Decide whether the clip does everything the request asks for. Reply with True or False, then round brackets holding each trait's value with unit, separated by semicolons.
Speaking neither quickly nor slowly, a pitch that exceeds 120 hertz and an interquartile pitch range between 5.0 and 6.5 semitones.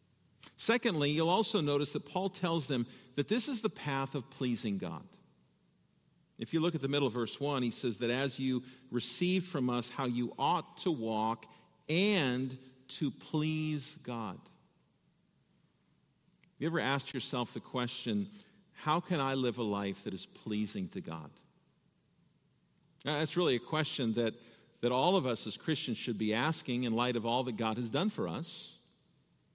True (175 wpm; 140 Hz; 5.4 semitones)